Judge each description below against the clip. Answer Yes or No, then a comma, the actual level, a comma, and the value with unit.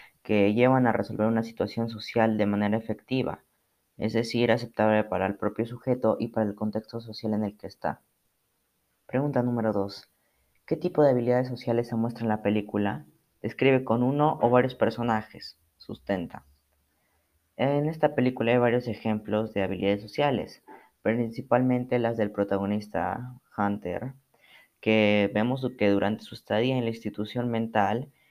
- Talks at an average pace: Yes, average, 150 wpm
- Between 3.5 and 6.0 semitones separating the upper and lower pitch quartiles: No, average, 2.9 semitones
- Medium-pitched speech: No, low, 110 Hz